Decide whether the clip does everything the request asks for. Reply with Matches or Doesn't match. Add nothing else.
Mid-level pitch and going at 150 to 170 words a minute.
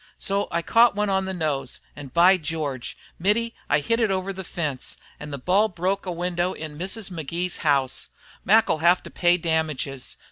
Doesn't match